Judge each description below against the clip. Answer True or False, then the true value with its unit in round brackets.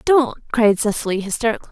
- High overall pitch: True (225 Hz)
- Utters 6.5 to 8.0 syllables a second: True (6.6 syllables/s)